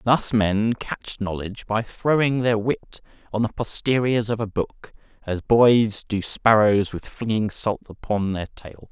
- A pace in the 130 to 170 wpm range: Yes, average, 160 wpm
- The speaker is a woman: No, male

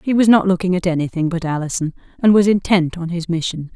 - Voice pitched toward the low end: No, medium, 180 Hz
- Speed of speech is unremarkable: No, fast, 225 wpm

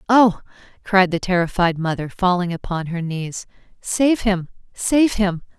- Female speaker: Yes, female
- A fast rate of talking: No, average, 140 wpm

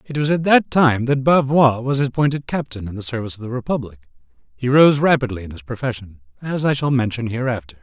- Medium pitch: No, low, 125 Hz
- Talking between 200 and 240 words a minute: Yes, fast, 205 wpm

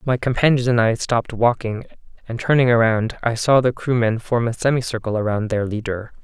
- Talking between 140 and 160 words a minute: No, average, 185 wpm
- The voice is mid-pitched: No, low, 115 Hz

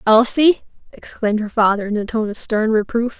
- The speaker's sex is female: Yes, female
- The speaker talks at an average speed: Yes, average, 190 wpm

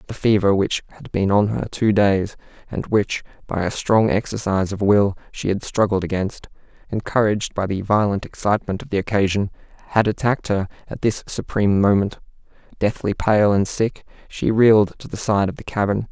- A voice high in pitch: No, low, 105 Hz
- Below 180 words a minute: Yes, average, 170 wpm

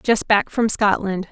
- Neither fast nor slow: Yes, average, 180 wpm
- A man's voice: No, female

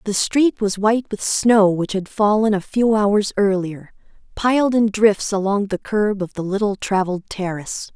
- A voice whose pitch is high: Yes, high, 205 Hz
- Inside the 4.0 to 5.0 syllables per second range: Yes, 4.6 syllables/s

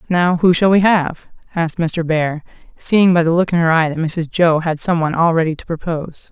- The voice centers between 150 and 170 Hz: Yes, medium, 165 Hz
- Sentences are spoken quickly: Yes, fast, 240 wpm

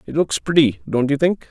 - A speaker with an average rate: No, fast, 240 wpm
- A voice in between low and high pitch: Yes, medium, 150 Hz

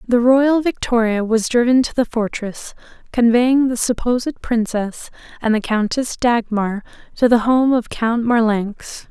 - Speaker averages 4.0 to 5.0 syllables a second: Yes, 4.2 syllables/s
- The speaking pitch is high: Yes, high, 235 Hz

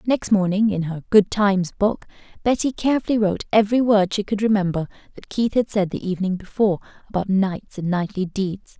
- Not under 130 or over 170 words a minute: No, average, 185 wpm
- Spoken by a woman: Yes, female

